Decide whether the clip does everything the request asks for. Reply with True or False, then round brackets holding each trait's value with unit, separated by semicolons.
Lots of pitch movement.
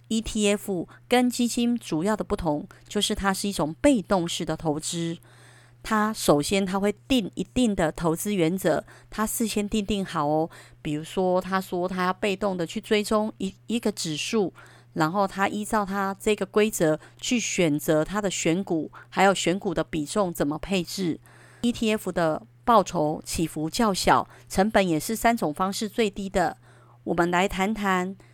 False (4.9 semitones)